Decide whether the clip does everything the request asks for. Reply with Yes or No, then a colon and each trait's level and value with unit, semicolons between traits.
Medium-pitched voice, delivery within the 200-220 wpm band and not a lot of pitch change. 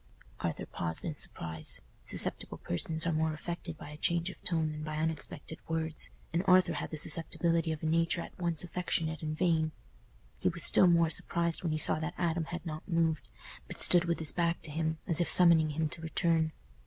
Yes: medium, 160 Hz; fast, 205 wpm; narrow, 1.5 semitones